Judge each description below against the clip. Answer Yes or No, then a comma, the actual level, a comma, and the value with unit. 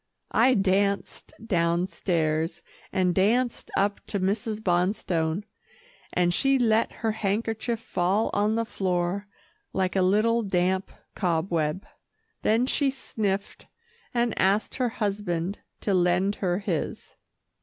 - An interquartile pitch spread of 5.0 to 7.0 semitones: No, average, 3.7 semitones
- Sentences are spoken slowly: Yes, slow, 115 wpm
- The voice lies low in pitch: No, high, 195 Hz